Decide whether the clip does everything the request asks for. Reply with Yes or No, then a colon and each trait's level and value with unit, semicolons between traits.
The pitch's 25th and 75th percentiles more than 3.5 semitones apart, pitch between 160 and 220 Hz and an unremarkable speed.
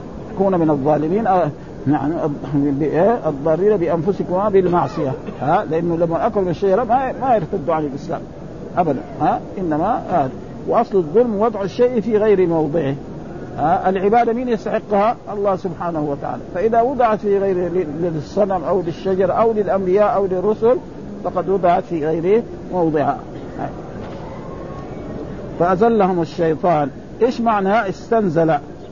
Yes: average, 4.3 semitones; medium, 185 Hz; average, 120 wpm